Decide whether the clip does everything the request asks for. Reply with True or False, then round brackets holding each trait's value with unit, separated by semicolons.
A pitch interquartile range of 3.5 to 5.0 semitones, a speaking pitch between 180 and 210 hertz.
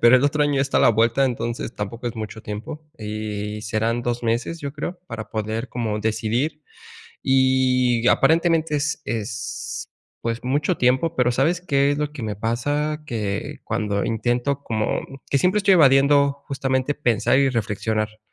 False (4.2 semitones; 125 Hz)